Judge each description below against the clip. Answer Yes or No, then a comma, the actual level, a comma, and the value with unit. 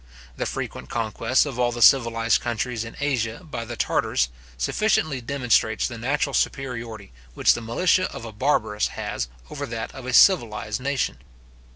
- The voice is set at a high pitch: No, low, 120 Hz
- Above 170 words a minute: No, average, 160 wpm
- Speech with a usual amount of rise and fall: Yes, average, 3.2 semitones